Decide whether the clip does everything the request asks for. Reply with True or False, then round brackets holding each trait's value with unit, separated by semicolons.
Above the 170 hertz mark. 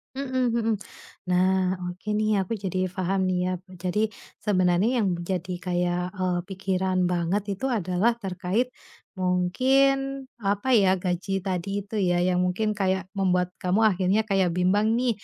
True (190 Hz)